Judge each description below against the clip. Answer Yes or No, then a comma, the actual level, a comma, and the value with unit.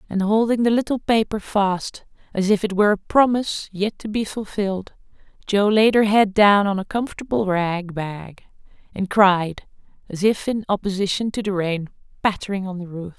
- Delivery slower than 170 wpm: No, average, 175 wpm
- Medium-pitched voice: No, high, 200 Hz